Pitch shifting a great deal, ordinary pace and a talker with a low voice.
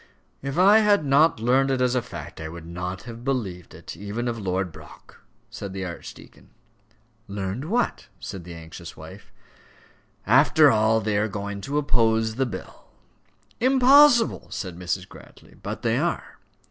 Yes: wide, 6.5 semitones; average, 155 wpm; low, 110 Hz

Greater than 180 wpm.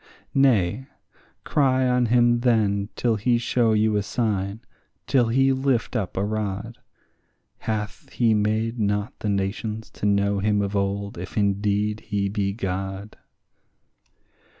No: slow, 135 wpm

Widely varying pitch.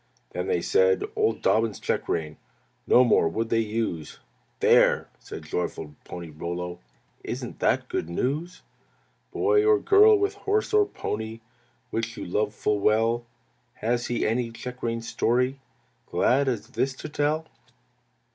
Yes: wide, 7.1 semitones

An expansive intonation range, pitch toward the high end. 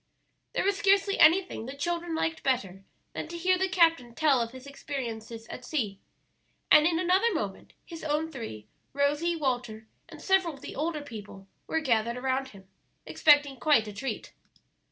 Yes: wide, 6.1 semitones; very high, 285 Hz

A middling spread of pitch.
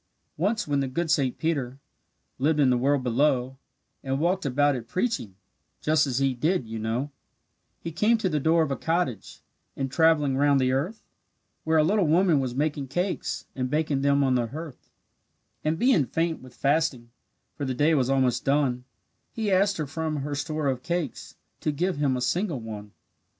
Yes: average, 3.9 semitones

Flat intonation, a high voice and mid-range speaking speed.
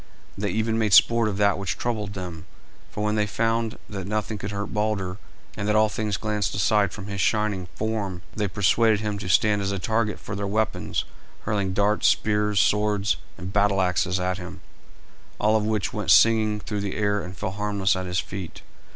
No: narrow, 1.7 semitones; low, 105 Hz; average, 195 wpm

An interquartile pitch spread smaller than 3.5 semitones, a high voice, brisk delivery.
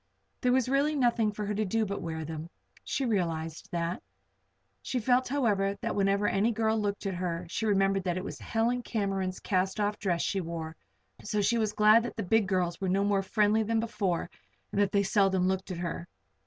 Yes: average, 3.1 semitones; high, 200 Hz; fast, 210 wpm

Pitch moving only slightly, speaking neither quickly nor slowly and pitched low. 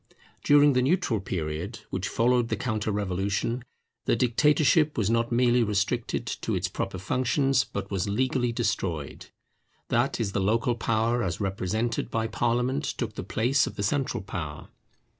No: average, 3.9 semitones; average, 155 wpm; low, 115 Hz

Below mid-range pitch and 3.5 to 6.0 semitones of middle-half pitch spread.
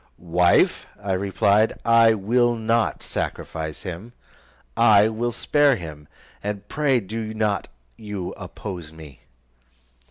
Yes: low, 105 Hz; average, 4.2 semitones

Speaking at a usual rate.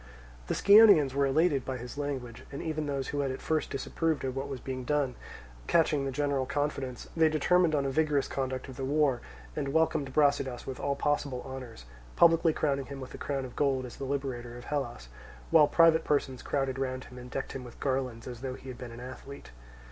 No: fast, 215 wpm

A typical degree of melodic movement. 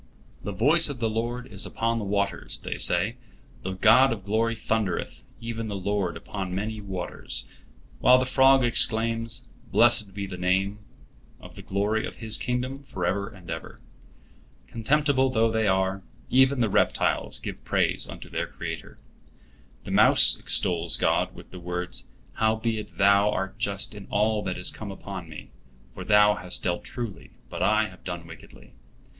Yes: average, 3.3 semitones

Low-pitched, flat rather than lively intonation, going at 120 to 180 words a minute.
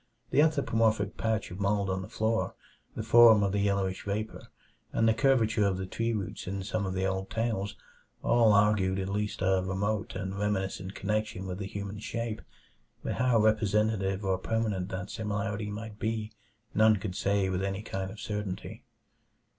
Yes: low, 105 Hz; narrow, 2.3 semitones; average, 175 wpm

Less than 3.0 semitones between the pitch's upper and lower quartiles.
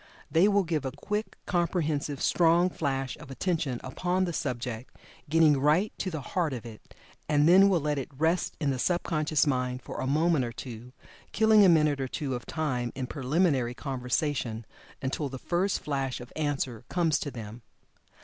No: average, 4.7 semitones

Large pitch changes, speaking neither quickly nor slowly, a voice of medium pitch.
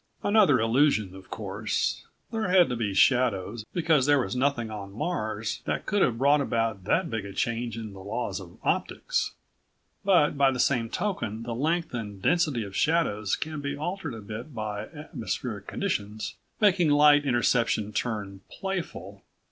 No: wide, 5.9 semitones; average, 165 wpm; low, 120 Hz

